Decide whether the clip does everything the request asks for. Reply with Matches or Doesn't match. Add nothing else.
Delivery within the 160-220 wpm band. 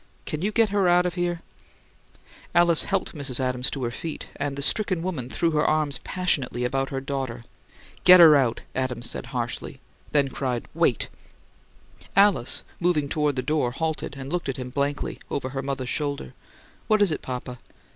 Matches